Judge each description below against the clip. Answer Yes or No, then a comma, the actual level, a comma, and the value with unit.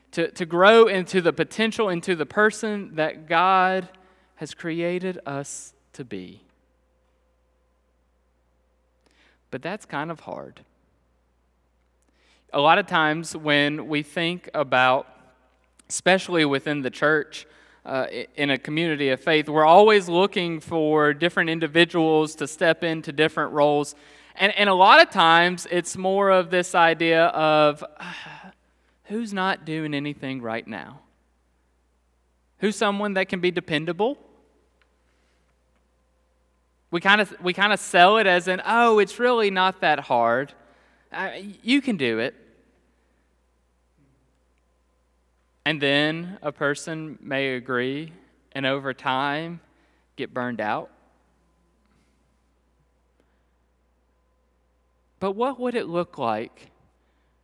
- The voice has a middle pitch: Yes, medium, 150 Hz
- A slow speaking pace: Yes, slow, 115 wpm